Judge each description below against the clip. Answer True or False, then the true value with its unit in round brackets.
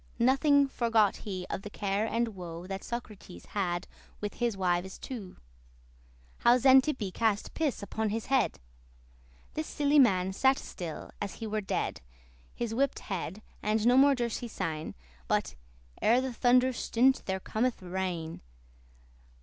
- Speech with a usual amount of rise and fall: True (4.8 semitones)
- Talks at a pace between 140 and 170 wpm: True (150 wpm)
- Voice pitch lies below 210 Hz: False (220 Hz)